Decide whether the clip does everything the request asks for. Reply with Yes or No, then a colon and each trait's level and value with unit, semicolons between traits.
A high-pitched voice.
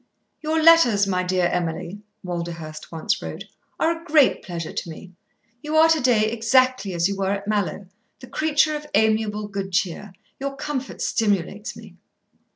Yes: high, 210 Hz